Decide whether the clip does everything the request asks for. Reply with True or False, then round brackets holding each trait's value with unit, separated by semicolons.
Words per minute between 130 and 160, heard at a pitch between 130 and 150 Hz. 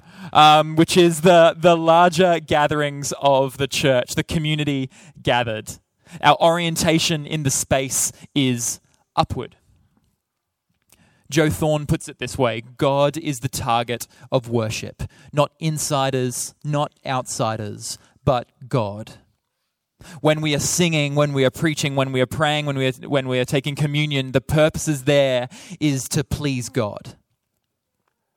True (140 wpm; 140 Hz)